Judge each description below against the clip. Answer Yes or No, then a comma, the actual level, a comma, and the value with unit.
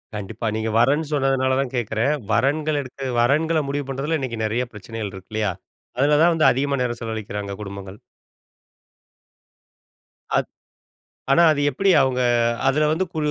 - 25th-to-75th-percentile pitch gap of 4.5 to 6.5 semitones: Yes, average, 4.8 semitones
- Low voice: Yes, low, 130 Hz